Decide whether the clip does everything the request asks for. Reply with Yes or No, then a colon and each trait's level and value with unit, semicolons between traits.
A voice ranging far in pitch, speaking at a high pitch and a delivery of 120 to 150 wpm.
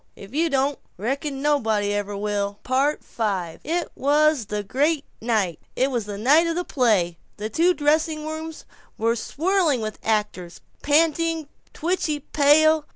Yes: wide, 6.7 semitones; very high, 275 Hz; average, 145 wpm